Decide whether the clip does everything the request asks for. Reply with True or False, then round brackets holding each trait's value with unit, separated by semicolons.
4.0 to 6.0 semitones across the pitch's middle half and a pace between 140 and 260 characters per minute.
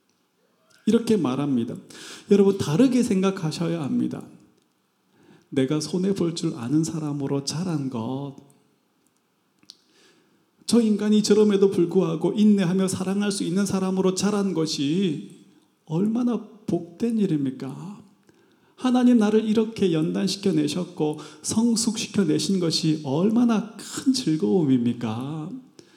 True (5.3 semitones; 250 characters per minute)